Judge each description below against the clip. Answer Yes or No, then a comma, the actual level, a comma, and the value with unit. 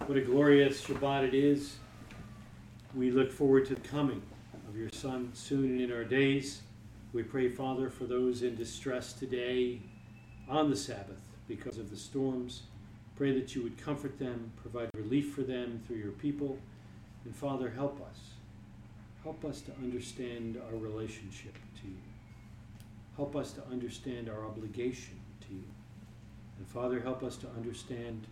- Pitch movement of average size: Yes, average, 3.1 semitones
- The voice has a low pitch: Yes, low, 120 Hz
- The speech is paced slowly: No, average, 155 wpm